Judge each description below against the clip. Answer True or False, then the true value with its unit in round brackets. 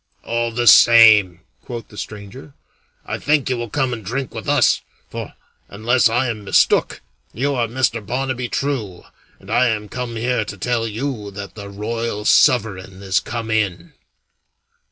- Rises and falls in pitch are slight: False (3.2 semitones)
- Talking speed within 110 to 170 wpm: True (160 wpm)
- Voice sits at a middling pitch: False (115 Hz)